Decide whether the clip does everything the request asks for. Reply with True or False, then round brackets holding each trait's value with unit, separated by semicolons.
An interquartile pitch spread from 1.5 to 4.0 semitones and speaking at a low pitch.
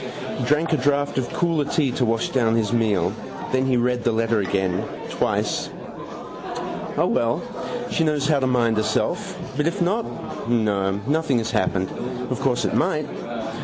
False (4.6 semitones; 125 Hz)